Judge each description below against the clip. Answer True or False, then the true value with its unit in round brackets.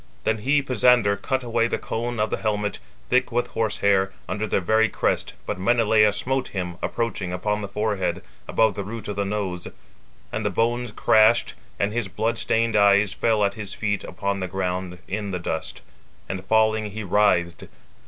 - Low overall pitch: True (105 Hz)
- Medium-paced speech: True (185 wpm)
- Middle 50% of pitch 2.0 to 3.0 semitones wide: True (2.5 semitones)